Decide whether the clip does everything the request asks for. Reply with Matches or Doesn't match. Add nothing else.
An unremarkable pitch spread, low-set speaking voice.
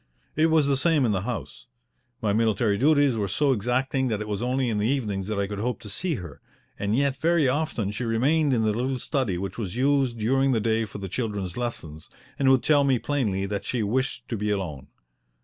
Matches